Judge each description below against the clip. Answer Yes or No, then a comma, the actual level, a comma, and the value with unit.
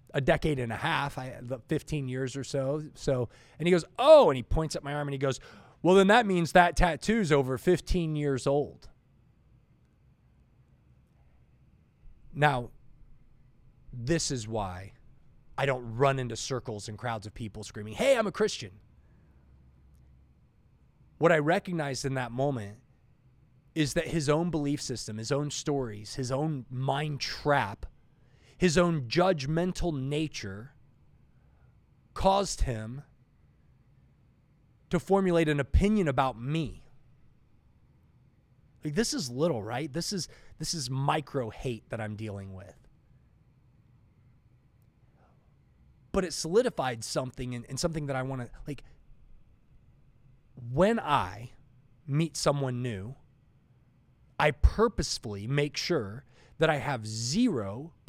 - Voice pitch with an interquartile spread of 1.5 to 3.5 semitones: No, average, 4.2 semitones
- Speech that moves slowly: Yes, slow, 125 wpm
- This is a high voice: No, low, 135 Hz